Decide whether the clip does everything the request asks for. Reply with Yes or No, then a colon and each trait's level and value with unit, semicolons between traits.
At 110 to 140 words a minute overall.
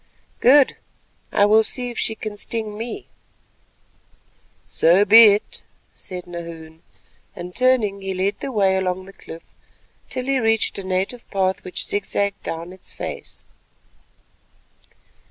Yes: slow, 135 wpm